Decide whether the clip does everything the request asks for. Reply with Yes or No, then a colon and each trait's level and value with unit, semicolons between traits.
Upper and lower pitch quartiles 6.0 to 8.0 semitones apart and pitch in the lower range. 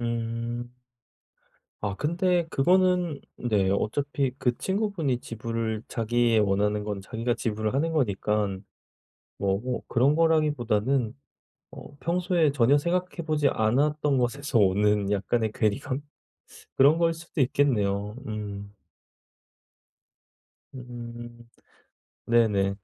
No: wide, 5.4 semitones; low, 120 Hz